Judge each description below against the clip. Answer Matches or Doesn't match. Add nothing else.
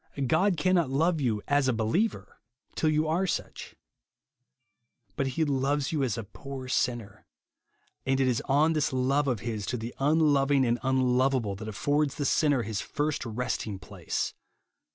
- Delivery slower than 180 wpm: Matches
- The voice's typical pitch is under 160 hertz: Matches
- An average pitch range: Matches